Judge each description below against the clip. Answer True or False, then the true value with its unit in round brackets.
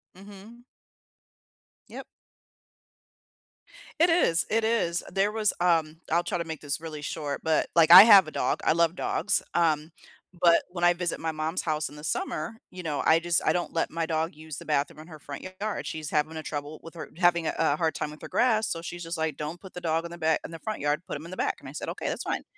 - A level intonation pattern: True (2.3 semitones)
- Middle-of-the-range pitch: True (165 Hz)